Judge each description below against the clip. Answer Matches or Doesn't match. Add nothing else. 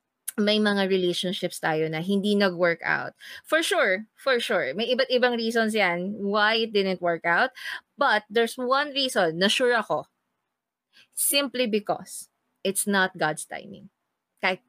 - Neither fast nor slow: Matches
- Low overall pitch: Doesn't match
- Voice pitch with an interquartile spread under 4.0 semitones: Doesn't match